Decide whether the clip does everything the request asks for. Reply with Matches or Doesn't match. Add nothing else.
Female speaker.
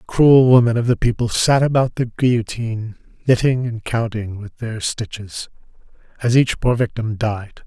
Doesn't match